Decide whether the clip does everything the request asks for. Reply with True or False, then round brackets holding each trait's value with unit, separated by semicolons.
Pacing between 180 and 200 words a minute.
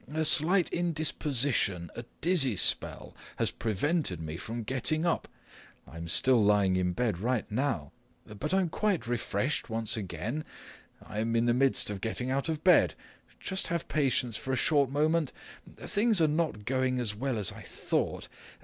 False (160 wpm)